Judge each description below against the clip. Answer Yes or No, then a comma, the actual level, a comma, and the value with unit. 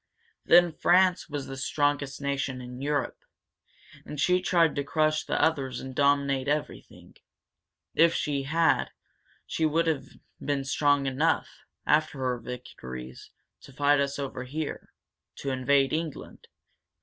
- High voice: No, medium, 145 Hz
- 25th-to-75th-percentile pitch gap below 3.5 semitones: Yes, narrow, 2.5 semitones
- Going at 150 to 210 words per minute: No, slow, 135 wpm